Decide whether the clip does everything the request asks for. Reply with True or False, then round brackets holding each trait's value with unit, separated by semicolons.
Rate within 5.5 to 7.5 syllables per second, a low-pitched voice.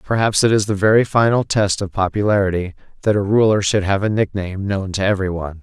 True (6.3 syllables/s; 100 Hz)